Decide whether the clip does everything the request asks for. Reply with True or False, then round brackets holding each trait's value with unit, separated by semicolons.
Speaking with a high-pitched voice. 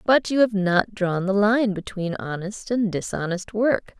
True (200 Hz)